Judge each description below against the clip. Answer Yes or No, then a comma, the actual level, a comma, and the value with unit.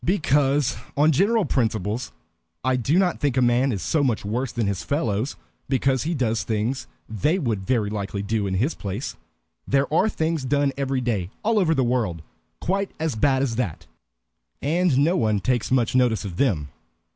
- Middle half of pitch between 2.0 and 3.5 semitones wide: No, average, 5.0 semitones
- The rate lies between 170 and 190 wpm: Yes, average, 180 wpm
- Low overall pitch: Yes, low, 130 Hz